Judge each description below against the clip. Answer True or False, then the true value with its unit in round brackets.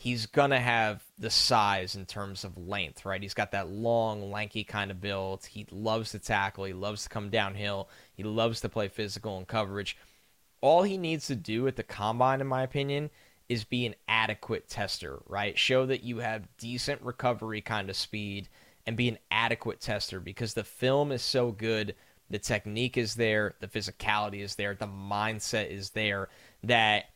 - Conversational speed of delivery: True (190 wpm)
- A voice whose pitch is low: True (110 Hz)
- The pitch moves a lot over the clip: False (3.2 semitones)